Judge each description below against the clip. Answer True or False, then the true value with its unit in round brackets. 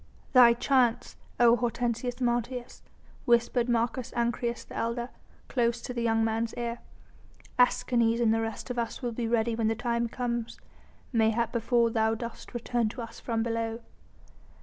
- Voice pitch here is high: True (235 Hz)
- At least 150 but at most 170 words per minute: True (155 wpm)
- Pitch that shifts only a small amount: True (1.0 semitones)